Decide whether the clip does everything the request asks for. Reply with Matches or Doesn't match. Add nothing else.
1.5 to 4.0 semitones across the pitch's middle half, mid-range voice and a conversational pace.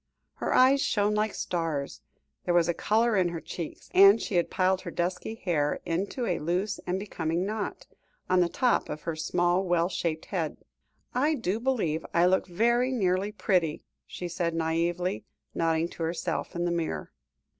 Matches